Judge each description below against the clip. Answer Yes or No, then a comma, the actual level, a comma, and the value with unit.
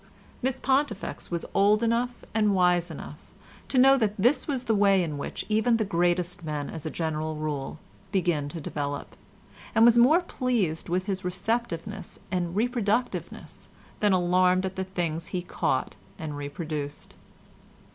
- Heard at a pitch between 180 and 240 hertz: Yes, medium, 185 Hz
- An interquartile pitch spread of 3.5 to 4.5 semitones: No, wide, 5.5 semitones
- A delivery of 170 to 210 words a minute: No, average, 155 wpm